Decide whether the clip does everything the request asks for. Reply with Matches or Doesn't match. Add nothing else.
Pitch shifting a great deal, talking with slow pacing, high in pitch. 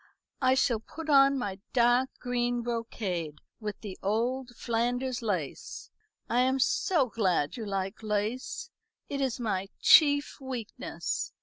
Doesn't match